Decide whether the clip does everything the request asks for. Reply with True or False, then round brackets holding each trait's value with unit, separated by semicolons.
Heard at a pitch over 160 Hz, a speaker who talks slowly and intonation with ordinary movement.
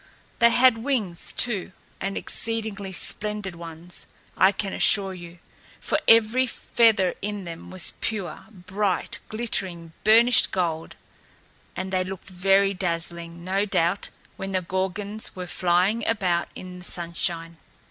True (190 Hz; 130 wpm; 3.3 semitones)